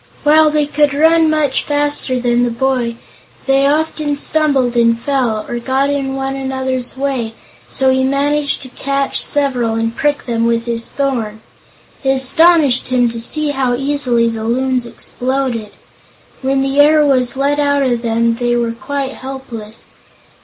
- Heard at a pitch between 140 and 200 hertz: No, very high, 265 Hz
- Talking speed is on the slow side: No, average, 160 wpm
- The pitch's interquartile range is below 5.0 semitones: Yes, average, 3.0 semitones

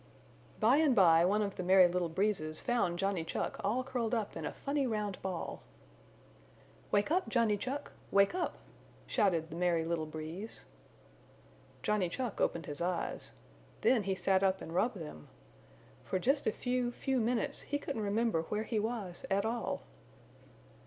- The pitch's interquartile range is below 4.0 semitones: No, average, 5.2 semitones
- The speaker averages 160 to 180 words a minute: Yes, average, 165 wpm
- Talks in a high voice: Yes, high, 205 Hz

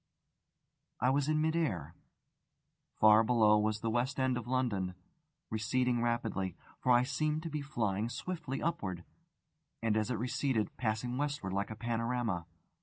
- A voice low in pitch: Yes, low, 120 Hz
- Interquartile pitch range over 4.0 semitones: No, average, 3.5 semitones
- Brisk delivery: No, average, 150 wpm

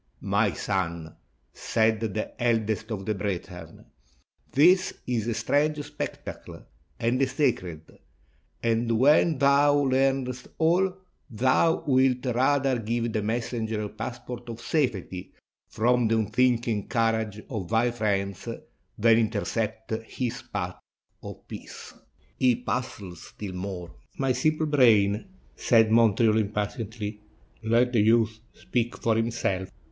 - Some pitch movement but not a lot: Yes, average, 3.1 semitones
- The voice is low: Yes, low, 115 Hz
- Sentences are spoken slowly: Yes, slow, 120 wpm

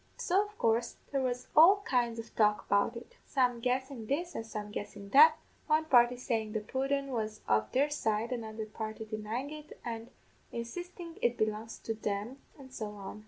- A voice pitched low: No, high, 235 Hz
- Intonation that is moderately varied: Yes, average, 4.2 semitones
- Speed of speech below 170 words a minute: No, average, 180 wpm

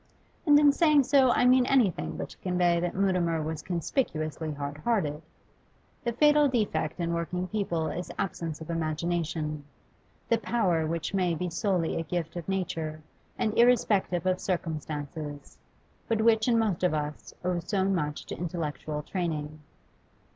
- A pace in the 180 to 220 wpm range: No, average, 155 wpm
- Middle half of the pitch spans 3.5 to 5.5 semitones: Yes, average, 5.1 semitones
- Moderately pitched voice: Yes, medium, 175 Hz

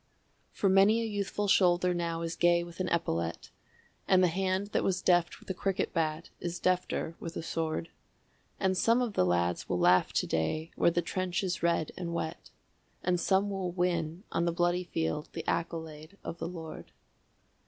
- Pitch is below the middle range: No, medium, 175 Hz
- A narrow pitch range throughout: Yes, narrow, 2.3 semitones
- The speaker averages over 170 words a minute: Yes, average, 185 wpm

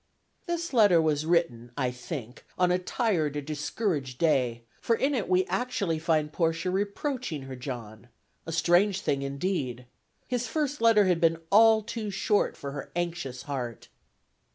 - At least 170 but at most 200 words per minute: No, average, 155 wpm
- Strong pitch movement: Yes, wide, 6.9 semitones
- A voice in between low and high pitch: Yes, medium, 165 Hz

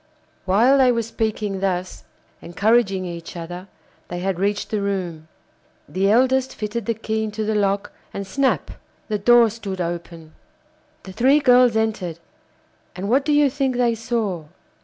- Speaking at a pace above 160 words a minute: No, average, 155 wpm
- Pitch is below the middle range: No, high, 210 Hz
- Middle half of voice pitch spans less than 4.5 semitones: Yes, average, 4.1 semitones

